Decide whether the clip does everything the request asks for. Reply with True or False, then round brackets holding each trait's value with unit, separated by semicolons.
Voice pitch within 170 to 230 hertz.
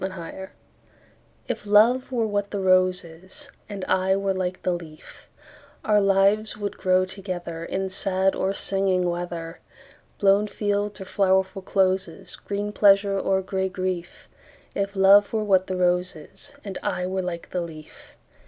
True (190 Hz)